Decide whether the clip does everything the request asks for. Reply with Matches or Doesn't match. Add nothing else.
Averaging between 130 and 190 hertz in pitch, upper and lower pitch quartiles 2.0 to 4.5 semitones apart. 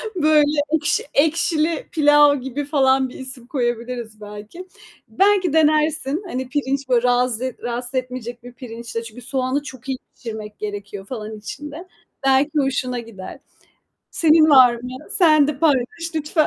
Doesn't match